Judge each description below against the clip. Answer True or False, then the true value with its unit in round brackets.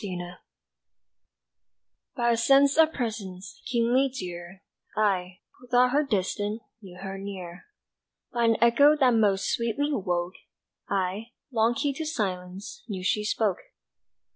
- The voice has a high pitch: True (215 Hz)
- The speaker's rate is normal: False (130 wpm)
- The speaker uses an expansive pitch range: False (4.7 semitones)